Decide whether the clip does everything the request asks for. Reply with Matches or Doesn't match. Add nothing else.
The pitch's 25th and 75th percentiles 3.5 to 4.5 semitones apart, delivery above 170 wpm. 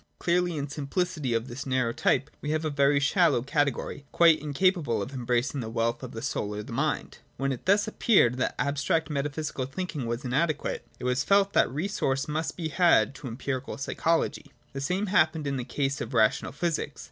Matches